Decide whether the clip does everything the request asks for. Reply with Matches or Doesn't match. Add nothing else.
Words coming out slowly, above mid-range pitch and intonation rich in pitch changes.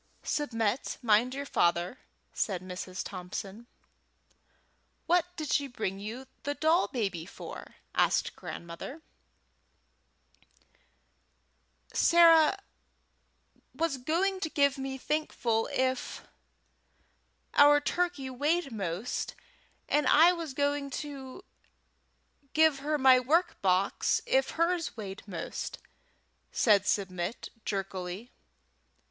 Matches